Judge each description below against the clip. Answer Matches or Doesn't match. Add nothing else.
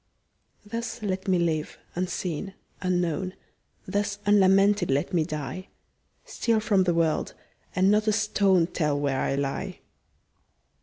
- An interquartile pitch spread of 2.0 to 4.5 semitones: Matches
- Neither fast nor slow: Doesn't match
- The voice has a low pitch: Doesn't match